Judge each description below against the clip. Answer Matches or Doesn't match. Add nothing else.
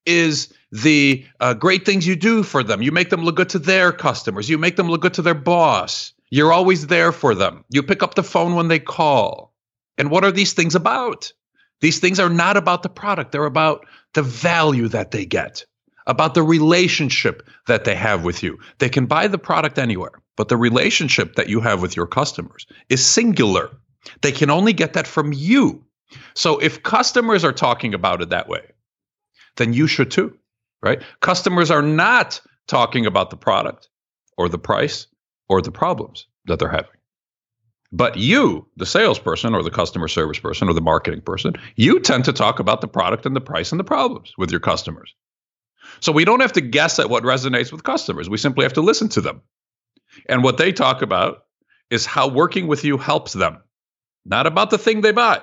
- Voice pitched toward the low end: Doesn't match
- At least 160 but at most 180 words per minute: Doesn't match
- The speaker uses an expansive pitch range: Matches